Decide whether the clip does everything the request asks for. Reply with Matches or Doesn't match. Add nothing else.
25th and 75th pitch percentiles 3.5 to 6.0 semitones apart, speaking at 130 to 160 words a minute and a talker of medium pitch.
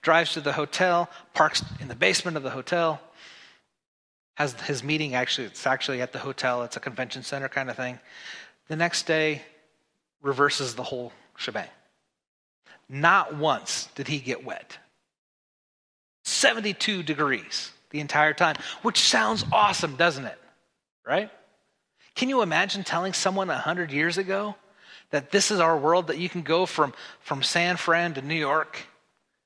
Matches